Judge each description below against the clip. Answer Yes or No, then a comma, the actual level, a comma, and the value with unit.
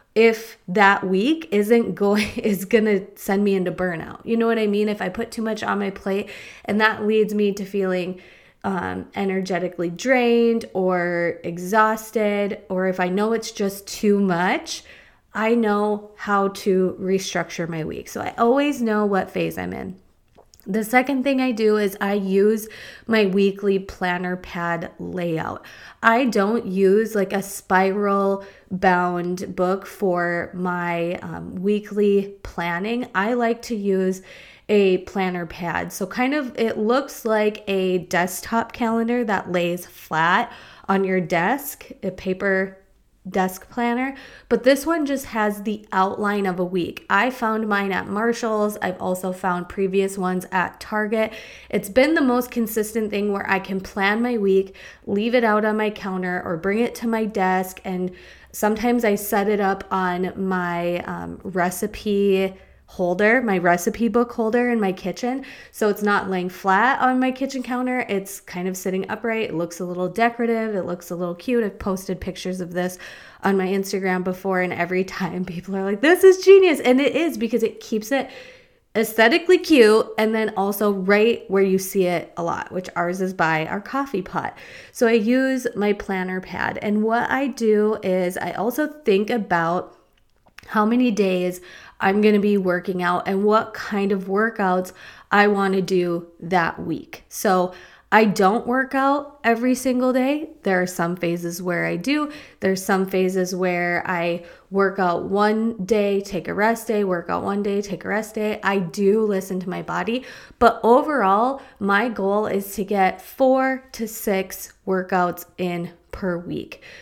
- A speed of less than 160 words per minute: No, average, 170 wpm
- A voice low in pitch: No, high, 200 Hz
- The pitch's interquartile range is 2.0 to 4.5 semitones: Yes, average, 3.4 semitones